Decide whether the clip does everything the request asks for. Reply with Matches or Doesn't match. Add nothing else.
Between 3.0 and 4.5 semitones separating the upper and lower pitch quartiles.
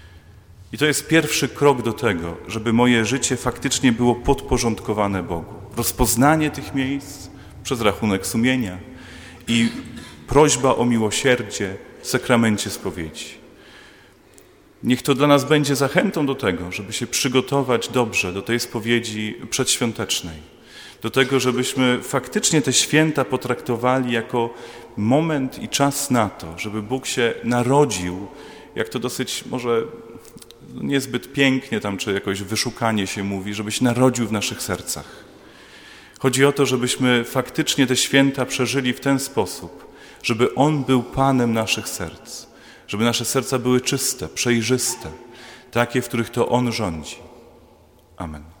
Matches